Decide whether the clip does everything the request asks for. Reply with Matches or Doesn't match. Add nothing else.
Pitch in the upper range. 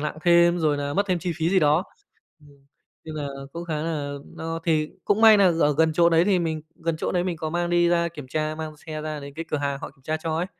Doesn't match